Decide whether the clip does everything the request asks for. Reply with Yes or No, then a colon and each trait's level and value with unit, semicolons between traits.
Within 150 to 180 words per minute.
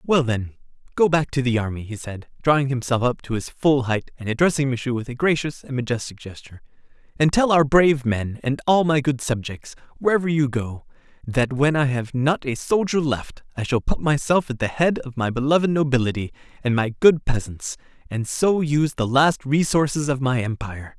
No: average, 200 wpm